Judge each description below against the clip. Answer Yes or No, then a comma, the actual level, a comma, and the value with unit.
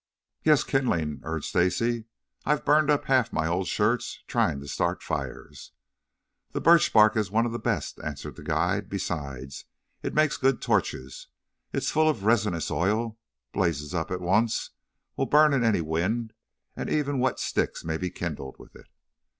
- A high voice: No, low, 105 Hz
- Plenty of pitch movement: Yes, wide, 6.9 semitones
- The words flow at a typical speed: Yes, average, 175 wpm